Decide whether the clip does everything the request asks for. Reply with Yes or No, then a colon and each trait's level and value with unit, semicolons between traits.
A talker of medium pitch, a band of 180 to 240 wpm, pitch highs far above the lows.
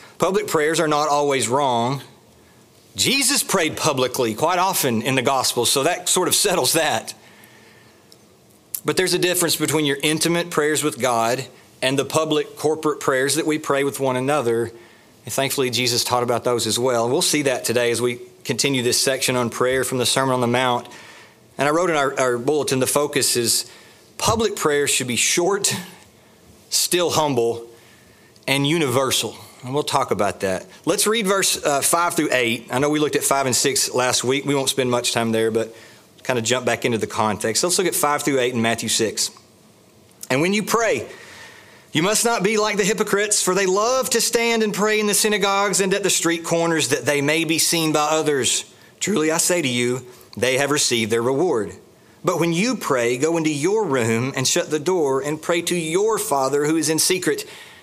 Yes: medium, 145 Hz; average, 200 wpm; wide, 5.7 semitones